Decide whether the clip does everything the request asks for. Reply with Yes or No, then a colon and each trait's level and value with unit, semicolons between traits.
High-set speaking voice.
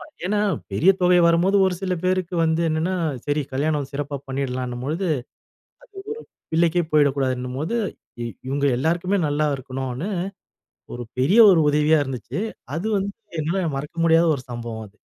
No: medium, 150 Hz